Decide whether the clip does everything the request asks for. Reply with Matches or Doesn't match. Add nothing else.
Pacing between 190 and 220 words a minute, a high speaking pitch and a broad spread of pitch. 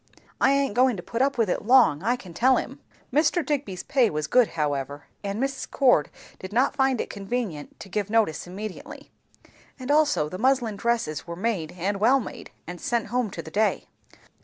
Matches